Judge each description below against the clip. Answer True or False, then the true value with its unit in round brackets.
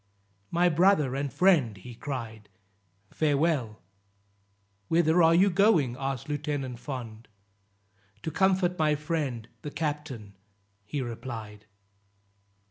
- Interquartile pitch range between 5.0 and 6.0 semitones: True (5.5 semitones)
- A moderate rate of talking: False (105 wpm)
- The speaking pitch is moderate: True (145 Hz)